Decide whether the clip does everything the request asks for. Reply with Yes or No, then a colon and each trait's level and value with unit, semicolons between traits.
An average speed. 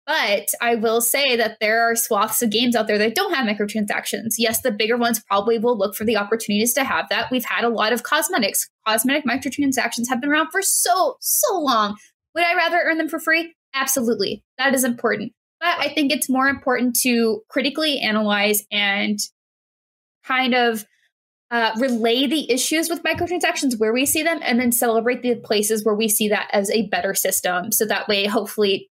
Yes: average, 195 wpm